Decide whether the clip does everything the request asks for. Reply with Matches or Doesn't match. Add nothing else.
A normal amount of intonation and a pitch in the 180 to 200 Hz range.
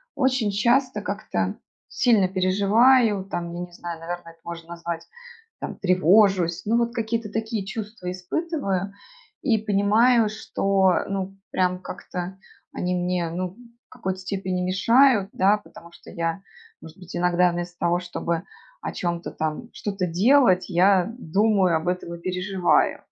Matches